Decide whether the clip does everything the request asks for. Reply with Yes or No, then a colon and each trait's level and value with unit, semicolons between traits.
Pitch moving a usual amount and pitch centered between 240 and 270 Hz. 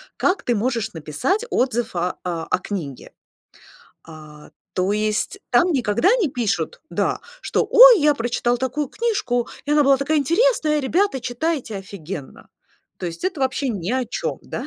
No: wide, 7.6 semitones; high, 245 Hz